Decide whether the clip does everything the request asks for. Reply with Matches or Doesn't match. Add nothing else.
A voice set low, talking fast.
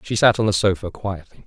Matches